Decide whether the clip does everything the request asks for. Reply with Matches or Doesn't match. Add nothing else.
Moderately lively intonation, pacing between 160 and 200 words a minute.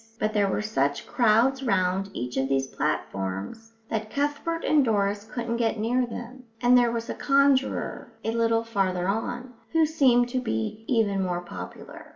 Matches